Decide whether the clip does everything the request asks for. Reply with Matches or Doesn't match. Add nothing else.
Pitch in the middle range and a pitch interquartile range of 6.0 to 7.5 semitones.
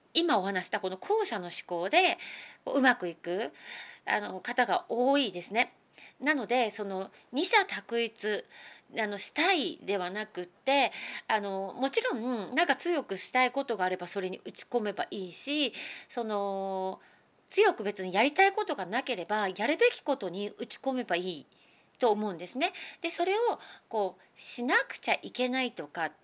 Doesn't match